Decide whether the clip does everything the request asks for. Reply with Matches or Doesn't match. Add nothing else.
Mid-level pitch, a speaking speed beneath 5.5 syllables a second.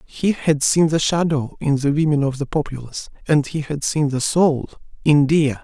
Matches